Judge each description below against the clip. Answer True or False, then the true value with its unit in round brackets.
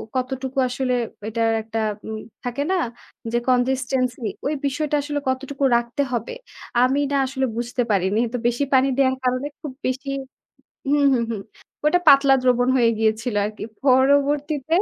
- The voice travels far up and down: False (2.5 semitones)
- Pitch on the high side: True (255 Hz)